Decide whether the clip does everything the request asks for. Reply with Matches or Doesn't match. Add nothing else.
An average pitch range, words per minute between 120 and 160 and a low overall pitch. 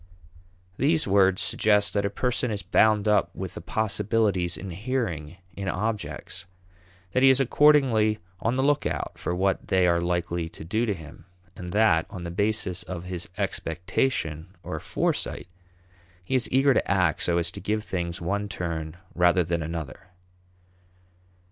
Matches